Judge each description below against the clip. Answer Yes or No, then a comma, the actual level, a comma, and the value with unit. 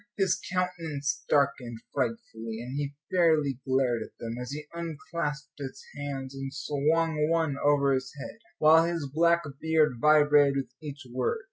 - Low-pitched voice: No, medium, 145 Hz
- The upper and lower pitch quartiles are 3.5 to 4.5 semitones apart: No, average, 3.1 semitones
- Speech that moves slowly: No, average, 150 wpm